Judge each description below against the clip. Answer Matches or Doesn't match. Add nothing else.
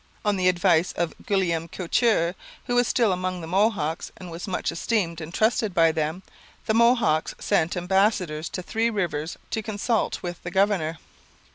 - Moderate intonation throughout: Matches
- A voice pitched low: Doesn't match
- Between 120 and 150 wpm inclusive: Doesn't match